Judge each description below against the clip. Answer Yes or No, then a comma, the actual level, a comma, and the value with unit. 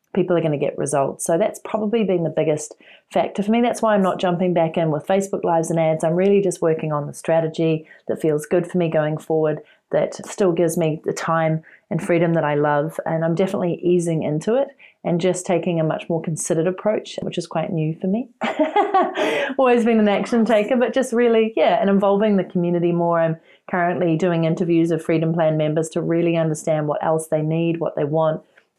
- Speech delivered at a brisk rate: Yes, fast, 215 wpm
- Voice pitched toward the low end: No, medium, 170 Hz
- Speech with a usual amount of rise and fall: Yes, average, 3.7 semitones